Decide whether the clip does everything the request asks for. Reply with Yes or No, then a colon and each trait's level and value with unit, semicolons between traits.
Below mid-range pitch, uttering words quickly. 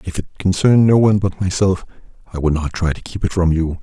Yes: very low, 90 Hz; fast, 250 wpm